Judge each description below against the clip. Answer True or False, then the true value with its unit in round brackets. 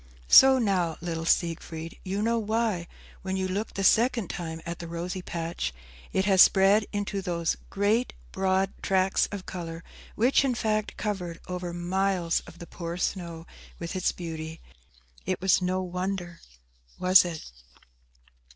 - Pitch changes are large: False (2.7 semitones)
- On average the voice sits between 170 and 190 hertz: True (185 Hz)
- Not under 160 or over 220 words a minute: False (150 wpm)